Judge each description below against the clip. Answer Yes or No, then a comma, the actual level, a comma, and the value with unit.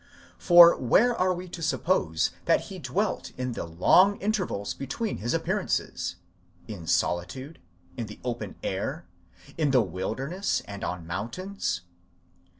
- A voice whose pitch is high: No, low, 130 Hz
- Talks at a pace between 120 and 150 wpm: Yes, average, 140 wpm